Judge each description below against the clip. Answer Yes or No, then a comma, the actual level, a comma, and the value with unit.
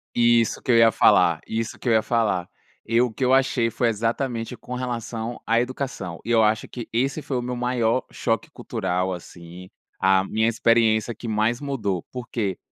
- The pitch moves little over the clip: Yes, narrow, 2.3 semitones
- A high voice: No, low, 115 Hz